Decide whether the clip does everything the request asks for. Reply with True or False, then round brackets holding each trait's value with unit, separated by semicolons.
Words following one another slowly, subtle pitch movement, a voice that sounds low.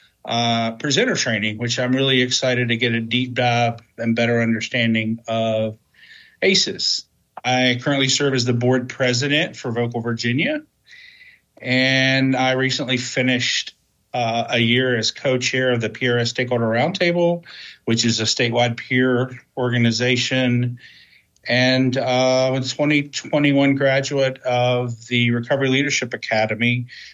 True (125 wpm; 1.9 semitones; 125 Hz)